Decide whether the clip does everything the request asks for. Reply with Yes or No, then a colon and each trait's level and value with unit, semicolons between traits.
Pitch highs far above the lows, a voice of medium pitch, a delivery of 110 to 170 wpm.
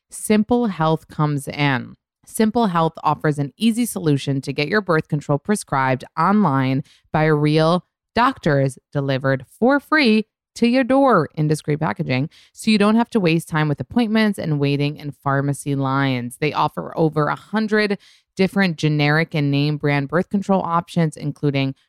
Yes: wide, 6.3 semitones; medium, 155 Hz; average, 155 wpm